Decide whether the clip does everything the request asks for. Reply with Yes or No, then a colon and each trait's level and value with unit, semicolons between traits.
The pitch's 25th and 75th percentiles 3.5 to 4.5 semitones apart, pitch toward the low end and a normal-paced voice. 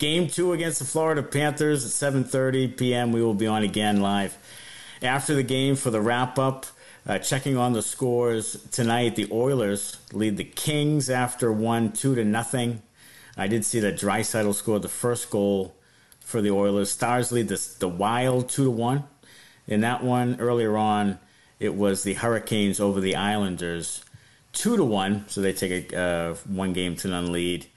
Yes: average, 4.1 semitones; low, 115 Hz; average, 180 wpm